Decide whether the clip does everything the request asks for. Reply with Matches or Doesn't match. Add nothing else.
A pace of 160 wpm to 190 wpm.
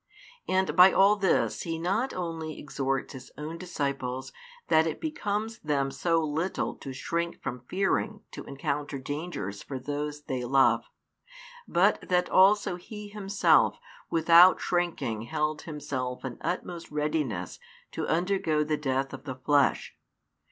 Doesn't match